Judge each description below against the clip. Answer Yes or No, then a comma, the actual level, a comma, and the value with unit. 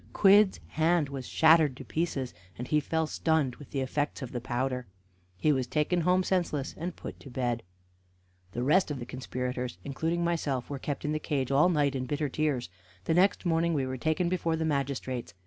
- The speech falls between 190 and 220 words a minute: Yes, average, 200 wpm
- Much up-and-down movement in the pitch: No, average, 3.9 semitones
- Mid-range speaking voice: Yes, medium, 145 Hz